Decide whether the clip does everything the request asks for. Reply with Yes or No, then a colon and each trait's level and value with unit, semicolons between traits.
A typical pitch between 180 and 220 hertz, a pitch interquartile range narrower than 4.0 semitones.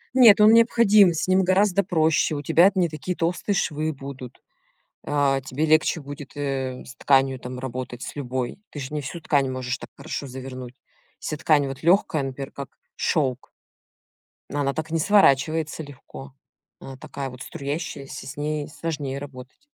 No: medium, 145 Hz; average, 3.5 semitones